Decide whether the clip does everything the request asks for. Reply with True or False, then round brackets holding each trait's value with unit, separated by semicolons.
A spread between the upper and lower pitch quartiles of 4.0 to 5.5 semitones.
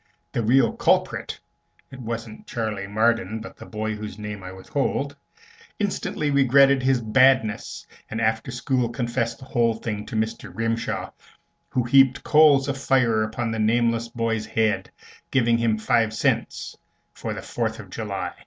False (2.9 semitones)